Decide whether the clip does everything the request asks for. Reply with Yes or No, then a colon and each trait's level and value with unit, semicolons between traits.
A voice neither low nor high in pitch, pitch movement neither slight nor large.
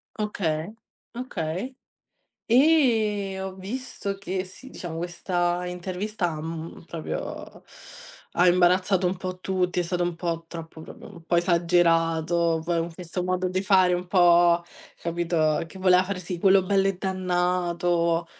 No: medium, 180 Hz; narrow, 1.9 semitones